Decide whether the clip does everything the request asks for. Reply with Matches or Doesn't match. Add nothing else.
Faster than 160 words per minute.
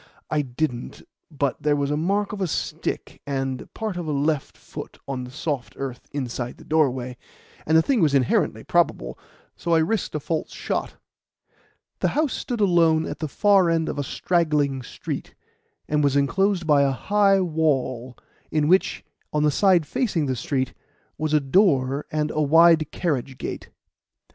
Matches